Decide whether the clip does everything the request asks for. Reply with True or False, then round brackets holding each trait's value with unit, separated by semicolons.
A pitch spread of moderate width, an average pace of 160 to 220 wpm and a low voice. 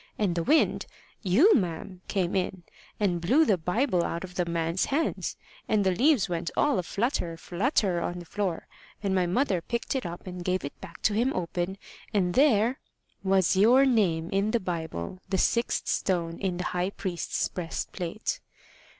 False (3.8 semitones; 175 wpm; 185 Hz)